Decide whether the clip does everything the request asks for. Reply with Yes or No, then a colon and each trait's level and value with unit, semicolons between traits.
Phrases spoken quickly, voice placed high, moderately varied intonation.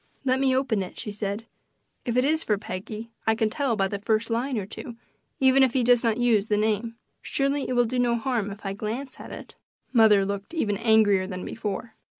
Yes: fast, 220 wpm; high, 225 Hz; average, 3.3 semitones